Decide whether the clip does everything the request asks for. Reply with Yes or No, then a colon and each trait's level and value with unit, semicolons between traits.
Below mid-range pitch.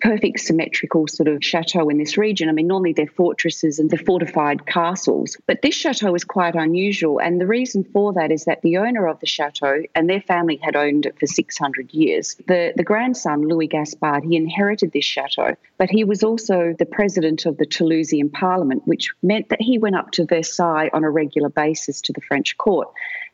No: medium, 170 Hz